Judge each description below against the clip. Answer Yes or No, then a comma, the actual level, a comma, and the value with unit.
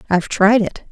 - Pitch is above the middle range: Yes, high, 205 Hz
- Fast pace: No, average, 195 wpm